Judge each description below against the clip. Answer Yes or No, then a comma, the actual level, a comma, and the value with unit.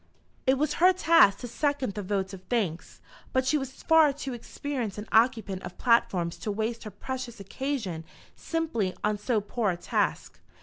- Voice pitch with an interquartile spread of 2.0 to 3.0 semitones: No, average, 5.2 semitones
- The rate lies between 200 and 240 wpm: No, average, 175 wpm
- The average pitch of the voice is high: Yes, high, 235 Hz